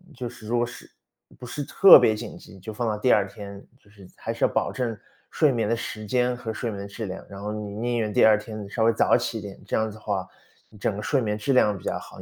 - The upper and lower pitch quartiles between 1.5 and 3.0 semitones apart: Yes, narrow, 2.5 semitones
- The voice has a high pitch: No, low, 110 Hz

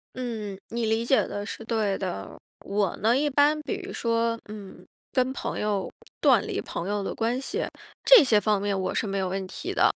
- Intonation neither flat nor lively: Yes, average, 4.0 semitones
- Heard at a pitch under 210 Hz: No, high, 220 Hz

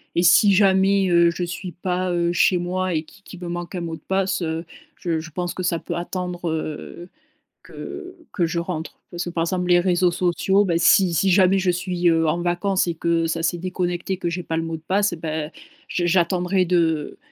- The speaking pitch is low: No, medium, 175 Hz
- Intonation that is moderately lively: No, narrow, 1.6 semitones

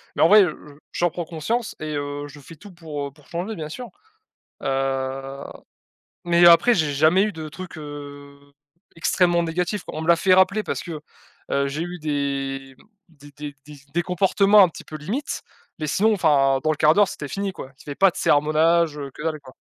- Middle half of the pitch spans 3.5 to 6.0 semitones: Yes, average, 3.8 semitones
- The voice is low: No, medium, 155 Hz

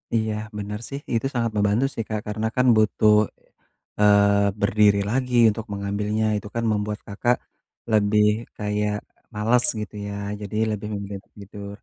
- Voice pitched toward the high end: No, low, 105 Hz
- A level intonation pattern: Yes, narrow, 1.2 semitones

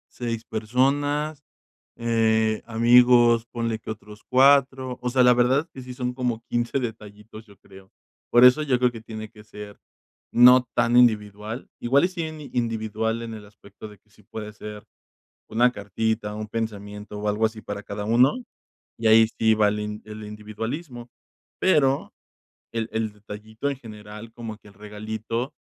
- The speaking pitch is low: Yes, low, 110 Hz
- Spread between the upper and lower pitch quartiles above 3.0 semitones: No, narrow, 2.6 semitones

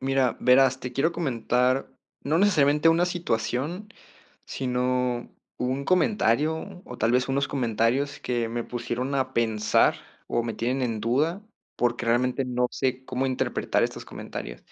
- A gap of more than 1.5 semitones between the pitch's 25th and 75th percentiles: Yes, average, 2.7 semitones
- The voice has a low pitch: Yes, low, 130 Hz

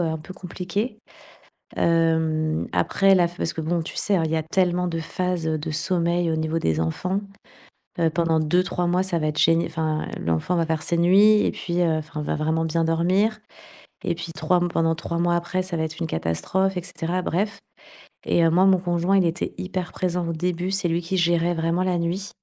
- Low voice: No, medium, 170 Hz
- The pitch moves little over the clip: Yes, narrow, 1.9 semitones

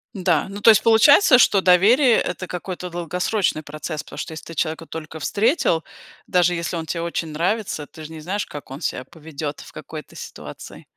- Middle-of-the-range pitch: Yes, medium, 170 Hz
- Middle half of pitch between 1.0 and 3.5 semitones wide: No, average, 4.1 semitones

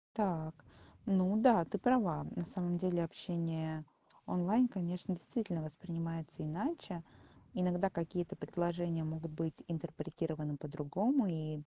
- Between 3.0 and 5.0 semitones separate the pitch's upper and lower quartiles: No, narrow, 2.6 semitones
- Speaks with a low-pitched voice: No, medium, 170 Hz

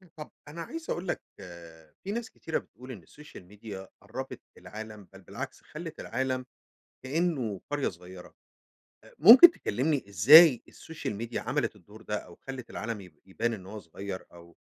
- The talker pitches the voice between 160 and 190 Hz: No, low, 120 Hz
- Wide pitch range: Yes, wide, 7.6 semitones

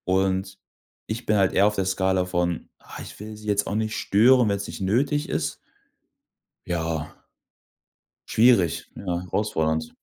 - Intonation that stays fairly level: No, average, 3.4 semitones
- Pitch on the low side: Yes, very low, 95 Hz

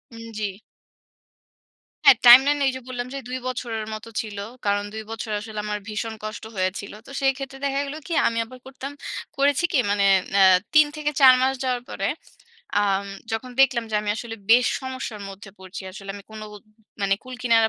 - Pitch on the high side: Yes, high, 230 Hz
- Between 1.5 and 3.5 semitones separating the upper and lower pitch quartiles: No, average, 3.9 semitones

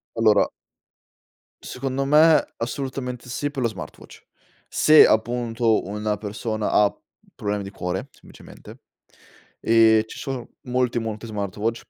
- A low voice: Yes, low, 115 Hz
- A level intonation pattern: No, average, 3.0 semitones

